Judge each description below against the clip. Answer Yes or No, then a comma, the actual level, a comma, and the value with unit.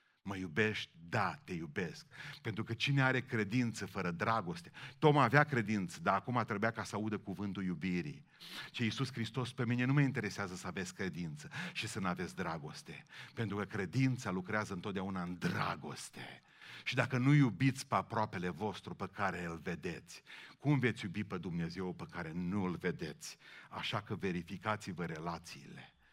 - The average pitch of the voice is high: No, low, 110 Hz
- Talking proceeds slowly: No, average, 165 wpm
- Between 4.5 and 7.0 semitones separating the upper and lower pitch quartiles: Yes, average, 4.9 semitones